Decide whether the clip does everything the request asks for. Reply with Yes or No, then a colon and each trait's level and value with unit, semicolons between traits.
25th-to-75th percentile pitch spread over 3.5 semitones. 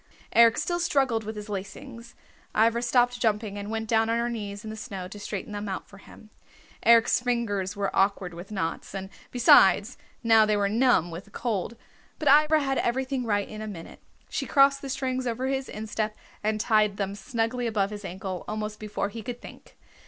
No: average, 3.0 semitones